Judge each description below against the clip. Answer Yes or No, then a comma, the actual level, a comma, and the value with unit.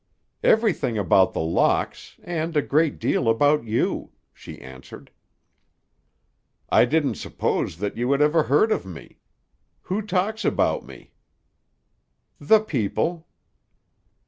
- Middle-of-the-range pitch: Yes, medium, 150 Hz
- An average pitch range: No, wide, 7.7 semitones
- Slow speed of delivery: Yes, slow, 120 wpm